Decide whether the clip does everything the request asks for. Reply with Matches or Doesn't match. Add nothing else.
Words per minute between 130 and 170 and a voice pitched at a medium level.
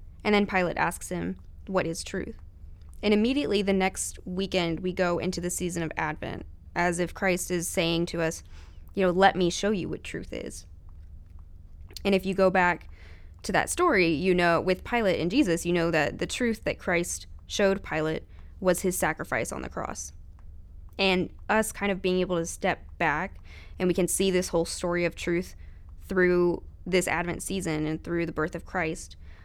Doesn't match